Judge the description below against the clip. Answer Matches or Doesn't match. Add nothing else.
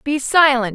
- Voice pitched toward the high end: Matches